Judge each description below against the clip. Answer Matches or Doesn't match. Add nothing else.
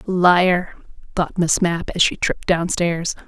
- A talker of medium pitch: Matches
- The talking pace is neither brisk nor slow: Matches